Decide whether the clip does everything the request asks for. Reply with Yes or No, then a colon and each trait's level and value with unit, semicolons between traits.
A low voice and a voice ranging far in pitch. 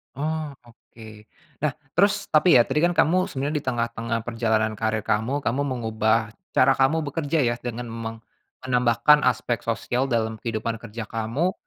No: low, 120 Hz; average, 4.2 semitones